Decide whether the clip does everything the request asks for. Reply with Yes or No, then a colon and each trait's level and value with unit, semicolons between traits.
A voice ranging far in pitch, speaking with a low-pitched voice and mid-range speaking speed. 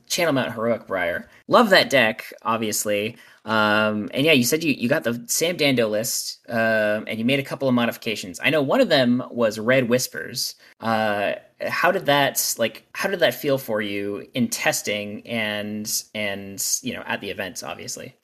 No: narrow, 2.5 semitones; low, 110 Hz; average, 190 wpm